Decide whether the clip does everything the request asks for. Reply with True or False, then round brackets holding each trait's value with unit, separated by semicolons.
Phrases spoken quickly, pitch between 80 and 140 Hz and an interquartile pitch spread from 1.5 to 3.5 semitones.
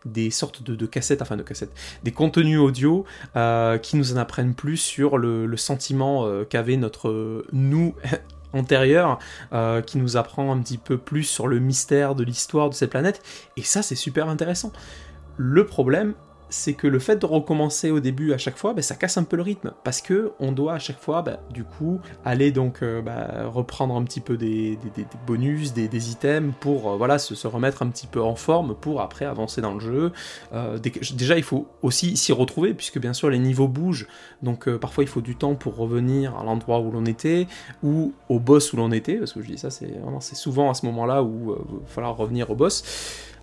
False (225 wpm; 135 Hz; 4.1 semitones)